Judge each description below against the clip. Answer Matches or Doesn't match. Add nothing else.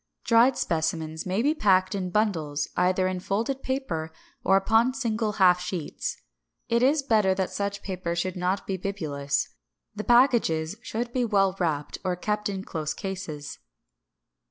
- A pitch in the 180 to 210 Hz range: Matches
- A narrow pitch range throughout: Doesn't match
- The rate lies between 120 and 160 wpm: Matches